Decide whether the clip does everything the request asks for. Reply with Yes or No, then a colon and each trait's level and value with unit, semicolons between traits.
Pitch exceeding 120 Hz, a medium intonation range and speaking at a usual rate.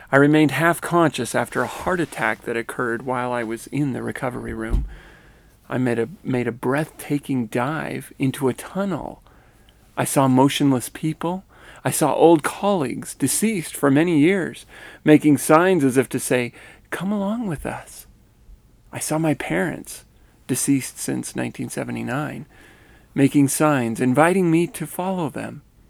Yes: medium, 140 Hz; average, 4.4 semitones; average, 145 wpm